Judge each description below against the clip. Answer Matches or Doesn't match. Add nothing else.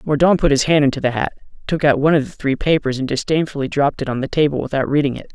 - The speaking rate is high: Matches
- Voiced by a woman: Doesn't match